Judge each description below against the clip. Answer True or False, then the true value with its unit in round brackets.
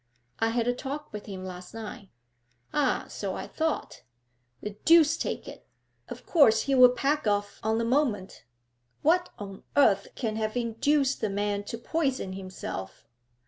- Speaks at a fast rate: False (155 wpm)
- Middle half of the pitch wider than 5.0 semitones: True (5.5 semitones)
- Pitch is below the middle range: False (225 Hz)